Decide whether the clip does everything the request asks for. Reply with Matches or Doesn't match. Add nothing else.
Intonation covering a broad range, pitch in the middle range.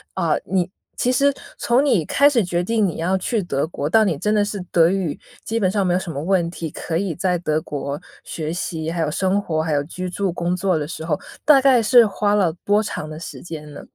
Doesn't match